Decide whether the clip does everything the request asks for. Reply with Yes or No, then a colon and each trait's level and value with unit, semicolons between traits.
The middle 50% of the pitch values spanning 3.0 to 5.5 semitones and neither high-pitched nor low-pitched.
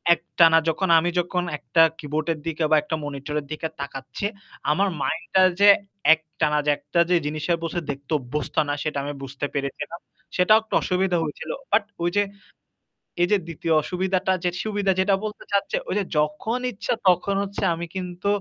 Yes: average, 4.0 semitones; medium, 170 Hz